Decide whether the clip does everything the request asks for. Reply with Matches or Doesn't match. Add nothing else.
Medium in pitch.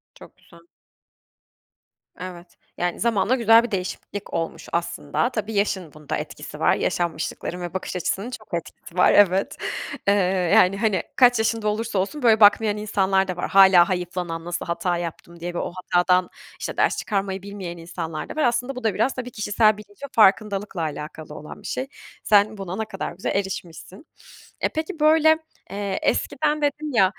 Doesn't match